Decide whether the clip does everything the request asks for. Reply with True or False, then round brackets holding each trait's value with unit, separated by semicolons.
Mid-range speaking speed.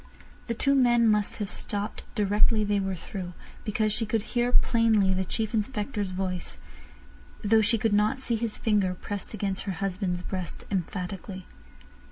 True (155 wpm)